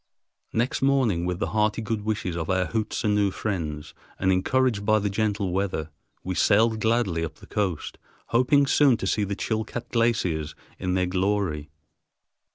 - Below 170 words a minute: Yes, average, 160 wpm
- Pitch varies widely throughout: No, average, 3.5 semitones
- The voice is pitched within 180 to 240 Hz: No, low, 100 Hz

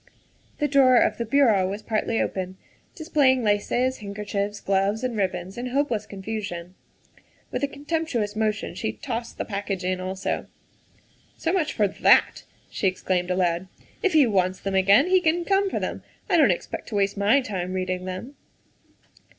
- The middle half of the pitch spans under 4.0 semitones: No, wide, 5.5 semitones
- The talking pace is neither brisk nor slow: Yes, average, 175 wpm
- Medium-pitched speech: No, high, 210 Hz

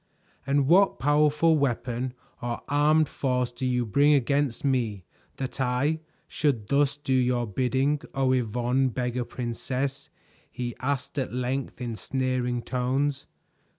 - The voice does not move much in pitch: Yes, narrow, 2.3 semitones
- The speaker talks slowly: Yes, slow, 130 wpm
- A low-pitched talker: Yes, low, 130 Hz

